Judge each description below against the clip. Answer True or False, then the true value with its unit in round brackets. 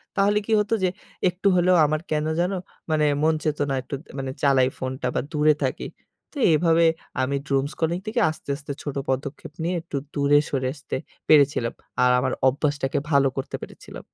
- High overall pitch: False (150 Hz)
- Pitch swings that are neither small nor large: True (3.3 semitones)